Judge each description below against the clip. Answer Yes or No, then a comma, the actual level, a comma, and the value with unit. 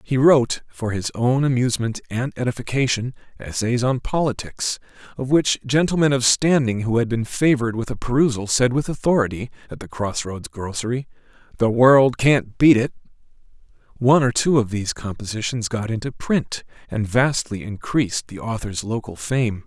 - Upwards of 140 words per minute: Yes, average, 160 wpm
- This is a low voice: Yes, low, 120 Hz